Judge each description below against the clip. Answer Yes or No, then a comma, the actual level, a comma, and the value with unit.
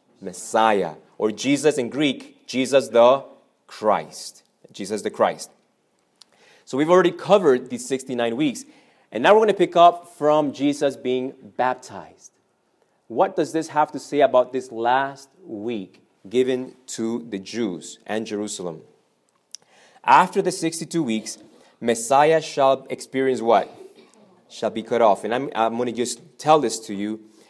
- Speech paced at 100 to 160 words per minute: Yes, average, 145 wpm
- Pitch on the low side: Yes, low, 130 Hz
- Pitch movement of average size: No, wide, 6.0 semitones